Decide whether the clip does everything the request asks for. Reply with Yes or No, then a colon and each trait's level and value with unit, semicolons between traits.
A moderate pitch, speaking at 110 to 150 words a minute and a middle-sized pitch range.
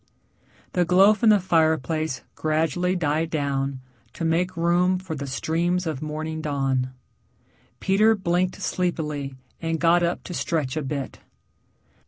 Yes: medium, 165 Hz; slow, 135 wpm; average, 3.2 semitones